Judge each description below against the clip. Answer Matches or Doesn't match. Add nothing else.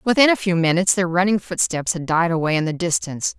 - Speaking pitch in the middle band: Matches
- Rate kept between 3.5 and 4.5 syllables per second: Doesn't match